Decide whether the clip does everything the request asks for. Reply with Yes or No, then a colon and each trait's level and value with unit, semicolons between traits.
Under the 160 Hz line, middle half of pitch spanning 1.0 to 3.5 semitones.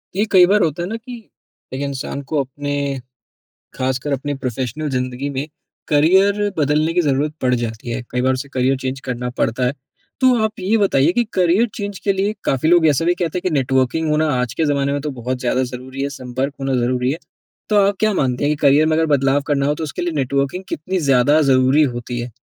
No: medium, 140 Hz; average, 4.2 semitones